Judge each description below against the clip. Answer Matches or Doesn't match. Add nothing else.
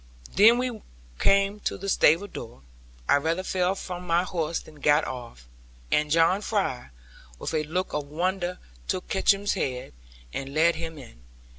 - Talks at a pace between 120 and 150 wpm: Doesn't match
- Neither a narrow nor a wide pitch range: Matches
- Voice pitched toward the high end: Doesn't match